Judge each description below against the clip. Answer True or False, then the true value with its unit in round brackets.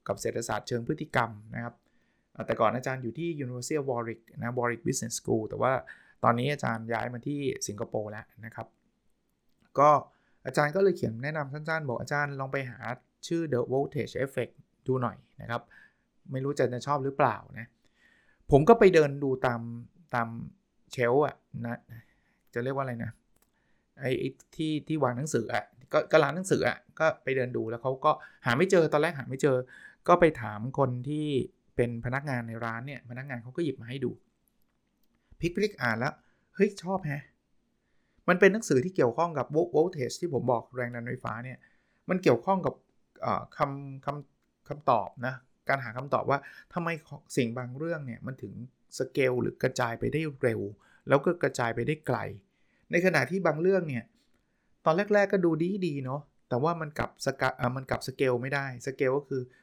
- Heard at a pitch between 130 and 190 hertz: True (135 Hz)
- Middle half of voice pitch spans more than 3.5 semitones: True (4.3 semitones)